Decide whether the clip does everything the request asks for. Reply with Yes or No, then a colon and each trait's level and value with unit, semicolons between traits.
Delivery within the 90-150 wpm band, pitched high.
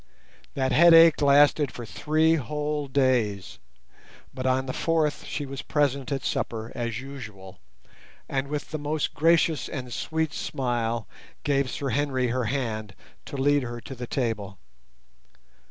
No: average, 140 wpm; low, 135 Hz